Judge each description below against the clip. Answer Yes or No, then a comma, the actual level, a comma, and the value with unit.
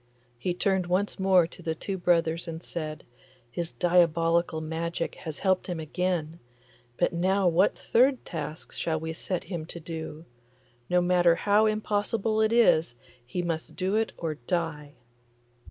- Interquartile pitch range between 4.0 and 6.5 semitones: No, average, 2.8 semitones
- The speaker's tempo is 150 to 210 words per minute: Yes, average, 155 wpm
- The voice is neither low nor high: Yes, medium, 175 Hz